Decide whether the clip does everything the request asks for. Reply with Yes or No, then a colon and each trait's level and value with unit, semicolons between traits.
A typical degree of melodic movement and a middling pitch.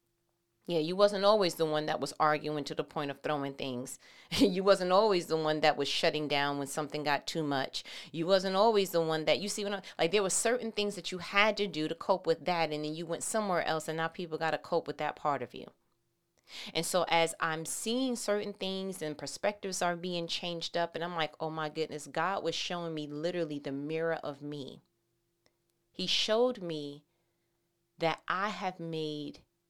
Yes: average, 3.8 semitones; medium, 165 Hz